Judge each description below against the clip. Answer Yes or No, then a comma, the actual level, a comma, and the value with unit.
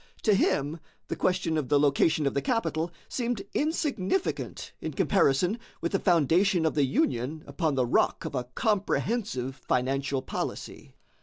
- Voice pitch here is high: No, medium, 160 Hz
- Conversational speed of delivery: Yes, average, 150 wpm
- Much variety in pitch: Yes, wide, 6.1 semitones